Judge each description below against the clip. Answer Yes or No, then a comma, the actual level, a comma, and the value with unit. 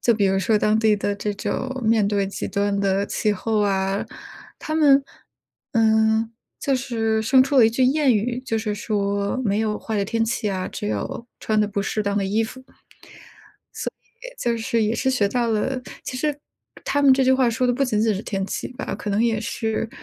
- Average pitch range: Yes, average, 3.3 semitones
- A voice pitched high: Yes, high, 220 Hz